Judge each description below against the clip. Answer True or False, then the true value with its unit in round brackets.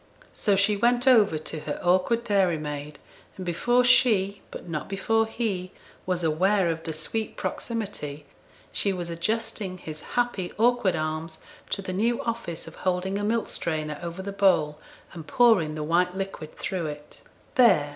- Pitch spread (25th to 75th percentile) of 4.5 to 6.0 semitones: True (5.3 semitones)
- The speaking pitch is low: False (185 Hz)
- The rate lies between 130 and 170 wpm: True (160 wpm)